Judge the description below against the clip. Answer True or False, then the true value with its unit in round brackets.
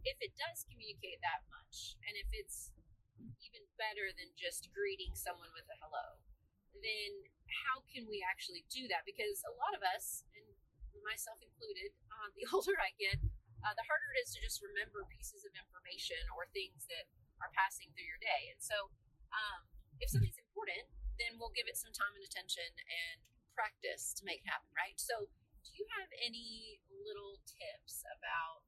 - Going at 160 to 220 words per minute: True (180 wpm)